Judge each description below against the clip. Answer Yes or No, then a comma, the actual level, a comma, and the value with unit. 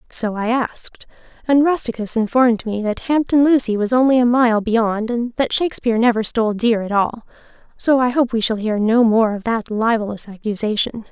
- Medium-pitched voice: No, high, 230 Hz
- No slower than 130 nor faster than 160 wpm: No, average, 190 wpm